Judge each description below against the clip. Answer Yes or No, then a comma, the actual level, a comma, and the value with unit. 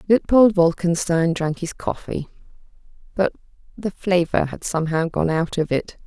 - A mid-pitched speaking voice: Yes, medium, 175 Hz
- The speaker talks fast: No, average, 140 wpm